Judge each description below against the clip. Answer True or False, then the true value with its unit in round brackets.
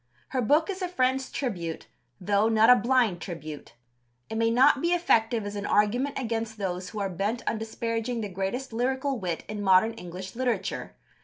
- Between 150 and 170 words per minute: False (180 wpm)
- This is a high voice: True (225 Hz)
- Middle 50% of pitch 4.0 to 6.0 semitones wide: True (4.4 semitones)